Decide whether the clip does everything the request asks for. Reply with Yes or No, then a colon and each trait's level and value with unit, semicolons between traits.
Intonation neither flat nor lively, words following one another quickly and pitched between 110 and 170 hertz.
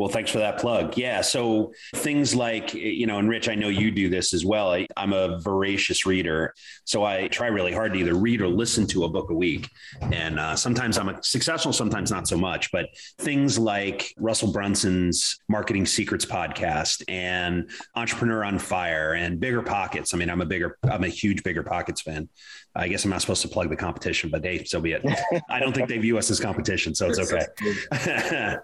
No: average, 4.0 semitones; fast, 210 wpm; low, 100 Hz